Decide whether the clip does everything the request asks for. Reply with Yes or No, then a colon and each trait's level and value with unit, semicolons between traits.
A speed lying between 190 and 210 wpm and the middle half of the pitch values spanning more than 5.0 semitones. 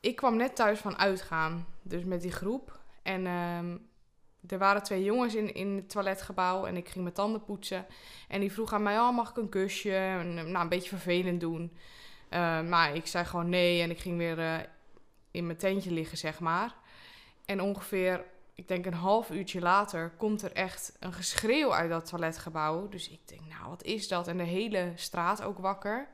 No: fast, 200 wpm; narrow, 2.6 semitones